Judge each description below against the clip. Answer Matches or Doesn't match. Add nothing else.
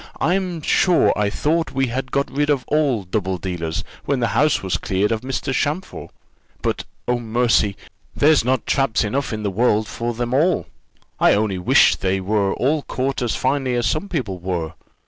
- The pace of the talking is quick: Doesn't match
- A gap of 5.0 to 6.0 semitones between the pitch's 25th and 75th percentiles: Matches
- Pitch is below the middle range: Matches